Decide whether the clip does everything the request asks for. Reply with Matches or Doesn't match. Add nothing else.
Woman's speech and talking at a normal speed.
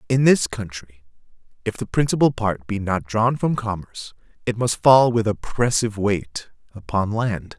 Doesn't match